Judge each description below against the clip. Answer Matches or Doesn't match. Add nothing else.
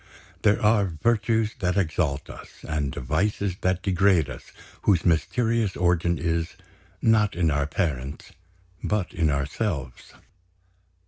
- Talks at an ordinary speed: Doesn't match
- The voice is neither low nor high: Doesn't match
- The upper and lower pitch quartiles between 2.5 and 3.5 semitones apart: Doesn't match